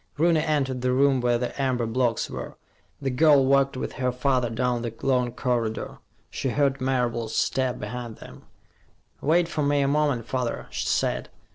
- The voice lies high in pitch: No, low, 130 Hz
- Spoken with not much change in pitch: Yes, narrow, 2.3 semitones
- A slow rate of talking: No, average, 170 wpm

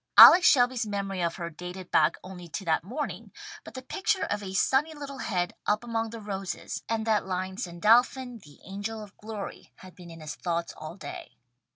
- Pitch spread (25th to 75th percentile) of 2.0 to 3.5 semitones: No, average, 4.6 semitones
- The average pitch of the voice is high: Yes, high, 200 Hz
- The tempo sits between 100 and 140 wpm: No, average, 195 wpm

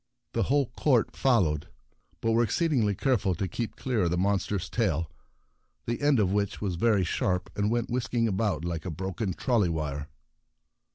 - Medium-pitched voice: No, low, 100 Hz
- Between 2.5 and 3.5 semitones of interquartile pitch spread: No, average, 4.9 semitones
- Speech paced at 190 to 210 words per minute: No, average, 170 wpm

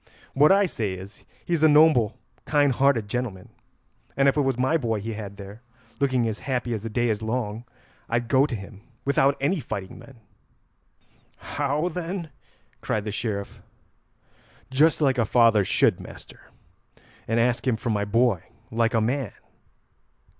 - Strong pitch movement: No, average, 4.5 semitones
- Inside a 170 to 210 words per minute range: No, average, 160 wpm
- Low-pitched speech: Yes, low, 120 Hz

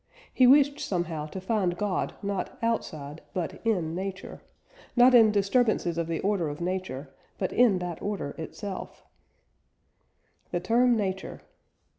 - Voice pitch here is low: No, high, 190 Hz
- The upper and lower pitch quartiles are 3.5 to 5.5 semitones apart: Yes, average, 4.2 semitones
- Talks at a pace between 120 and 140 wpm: Yes, slow, 135 wpm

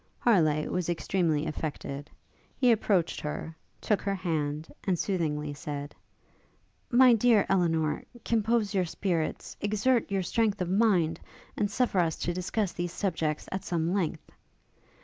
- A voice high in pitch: No, medium, 180 Hz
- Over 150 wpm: No, slow, 135 wpm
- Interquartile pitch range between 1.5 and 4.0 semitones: No, average, 4.4 semitones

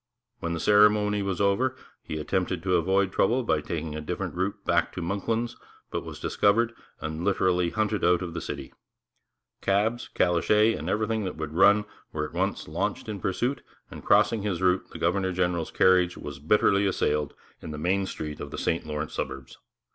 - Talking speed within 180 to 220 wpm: Yes, average, 185 wpm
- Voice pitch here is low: Yes, very low, 95 Hz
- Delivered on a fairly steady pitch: No, average, 3.8 semitones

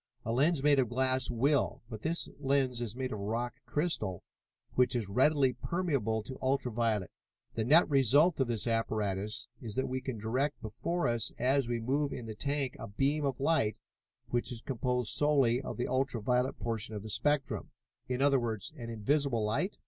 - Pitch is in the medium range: No, low, 125 Hz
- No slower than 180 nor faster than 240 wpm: Yes, average, 185 wpm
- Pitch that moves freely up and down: No, average, 3.6 semitones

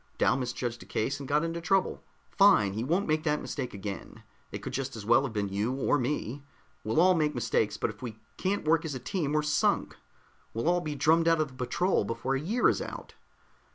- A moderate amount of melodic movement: No, wide, 5.8 semitones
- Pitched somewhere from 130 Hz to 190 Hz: Yes, medium, 140 Hz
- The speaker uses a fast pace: Yes, fast, 225 wpm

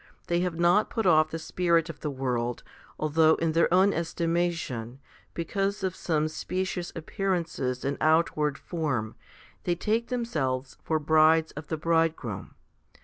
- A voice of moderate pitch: Yes, medium, 165 Hz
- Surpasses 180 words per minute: No, average, 145 wpm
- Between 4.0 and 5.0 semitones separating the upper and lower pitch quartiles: No, narrow, 2.6 semitones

